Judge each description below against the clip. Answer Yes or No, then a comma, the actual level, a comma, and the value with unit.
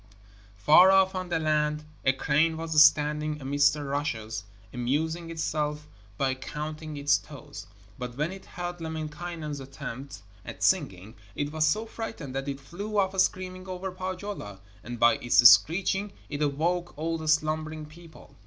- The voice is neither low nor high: Yes, medium, 155 Hz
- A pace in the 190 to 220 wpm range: No, average, 155 wpm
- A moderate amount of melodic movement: Yes, average, 3.5 semitones